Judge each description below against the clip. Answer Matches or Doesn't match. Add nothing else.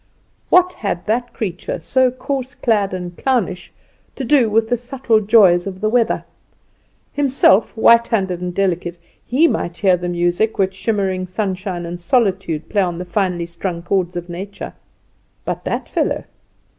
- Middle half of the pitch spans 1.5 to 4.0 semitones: Doesn't match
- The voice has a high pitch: Matches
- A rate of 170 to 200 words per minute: Doesn't match